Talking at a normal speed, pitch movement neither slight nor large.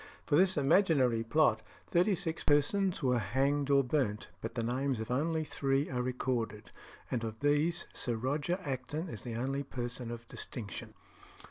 Yes: average, 160 wpm; average, 4.0 semitones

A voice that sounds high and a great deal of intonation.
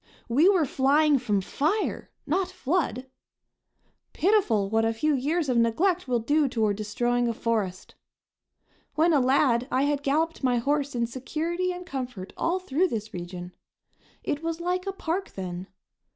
Yes: very high, 275 Hz; wide, 6.3 semitones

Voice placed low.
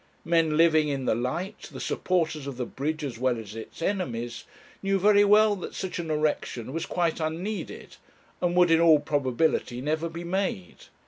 No: medium, 160 Hz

